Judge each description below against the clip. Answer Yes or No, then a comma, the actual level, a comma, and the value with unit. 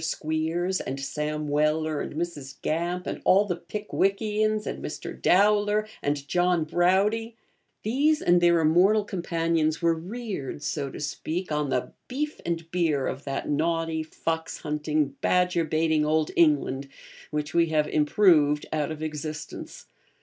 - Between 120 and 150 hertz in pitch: No, medium, 165 Hz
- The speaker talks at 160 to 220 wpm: No, average, 140 wpm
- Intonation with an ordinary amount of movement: Yes, average, 3.1 semitones